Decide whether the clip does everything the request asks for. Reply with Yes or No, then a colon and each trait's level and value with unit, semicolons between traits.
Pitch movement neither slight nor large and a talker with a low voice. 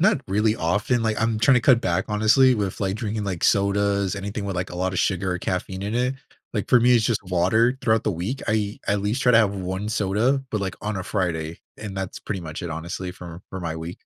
Yes: average, 3.1 semitones; low, 100 Hz